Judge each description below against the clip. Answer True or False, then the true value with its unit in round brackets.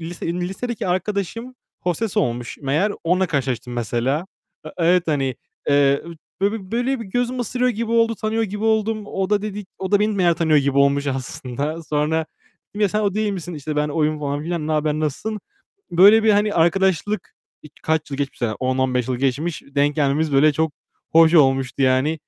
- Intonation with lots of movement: True (6.3 semitones)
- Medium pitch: True (165 Hz)